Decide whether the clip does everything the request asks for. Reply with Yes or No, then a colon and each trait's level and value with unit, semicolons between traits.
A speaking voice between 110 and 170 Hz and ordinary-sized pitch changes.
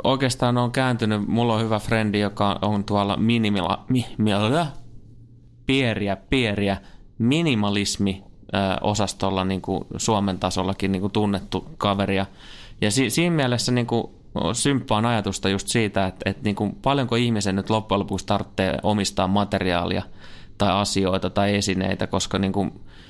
No: low, 100 Hz; average, 3.1 semitones